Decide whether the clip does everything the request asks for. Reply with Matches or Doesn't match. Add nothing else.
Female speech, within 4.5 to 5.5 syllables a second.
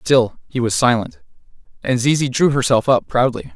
Doesn't match